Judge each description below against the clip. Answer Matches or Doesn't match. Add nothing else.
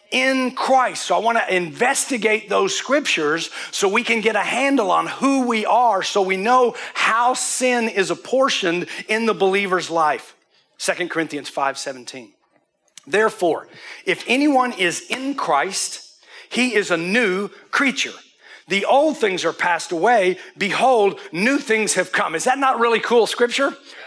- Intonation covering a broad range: Matches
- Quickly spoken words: Doesn't match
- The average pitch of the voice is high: Matches